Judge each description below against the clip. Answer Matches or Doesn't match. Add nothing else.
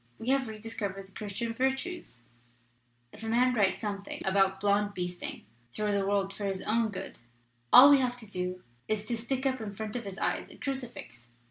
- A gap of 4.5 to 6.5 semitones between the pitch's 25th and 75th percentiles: Doesn't match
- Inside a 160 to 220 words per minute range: Matches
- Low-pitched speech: Doesn't match